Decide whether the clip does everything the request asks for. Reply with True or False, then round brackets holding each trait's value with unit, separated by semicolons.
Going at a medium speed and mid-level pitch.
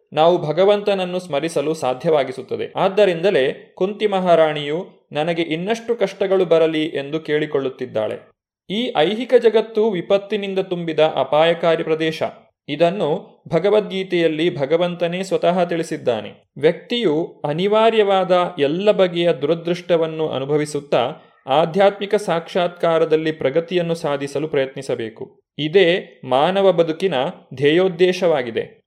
True (85 wpm; 170 Hz)